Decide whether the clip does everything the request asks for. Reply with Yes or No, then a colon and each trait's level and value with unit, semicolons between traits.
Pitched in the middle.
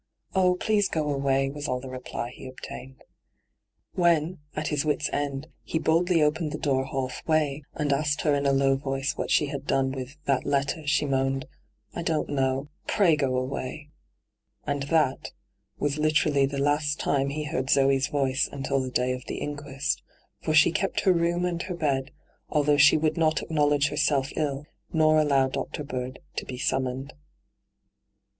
Yes: medium, 145 Hz